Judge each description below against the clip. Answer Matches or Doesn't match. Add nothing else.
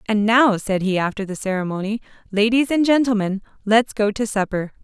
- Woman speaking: Matches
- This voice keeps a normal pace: Matches